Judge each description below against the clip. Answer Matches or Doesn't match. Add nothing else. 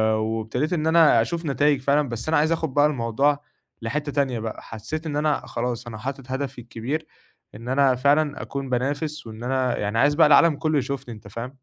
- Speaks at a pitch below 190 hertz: Matches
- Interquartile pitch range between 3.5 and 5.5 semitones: Matches